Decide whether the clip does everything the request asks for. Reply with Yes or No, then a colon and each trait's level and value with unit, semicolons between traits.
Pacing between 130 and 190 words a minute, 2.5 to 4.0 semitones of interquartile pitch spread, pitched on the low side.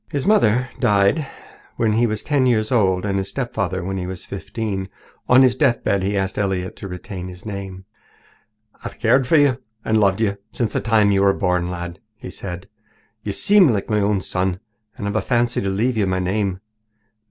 No: average, 200 wpm; average, 3.6 semitones; low, 100 Hz